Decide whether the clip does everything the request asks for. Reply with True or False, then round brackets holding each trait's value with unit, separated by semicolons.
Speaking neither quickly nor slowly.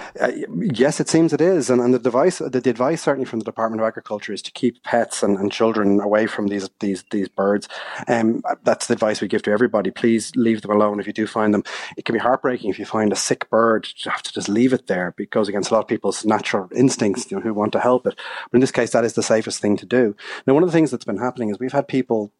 False (285 wpm)